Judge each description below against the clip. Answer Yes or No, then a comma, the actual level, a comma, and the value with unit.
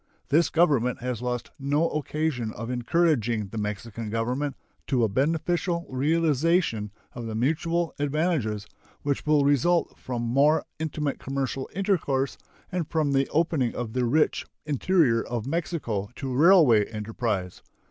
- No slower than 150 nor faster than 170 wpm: No, slow, 135 wpm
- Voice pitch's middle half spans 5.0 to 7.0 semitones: Yes, average, 5.3 semitones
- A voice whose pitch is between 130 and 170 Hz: Yes, low, 135 Hz